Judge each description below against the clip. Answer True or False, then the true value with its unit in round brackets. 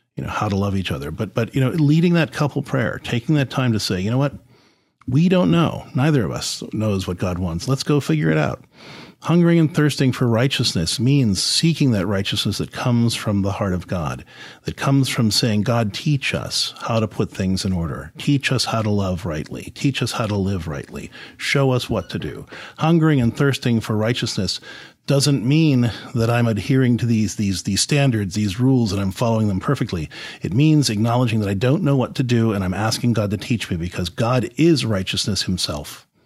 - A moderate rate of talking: False (210 wpm)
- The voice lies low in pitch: True (115 Hz)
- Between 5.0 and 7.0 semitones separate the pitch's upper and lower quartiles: True (5.4 semitones)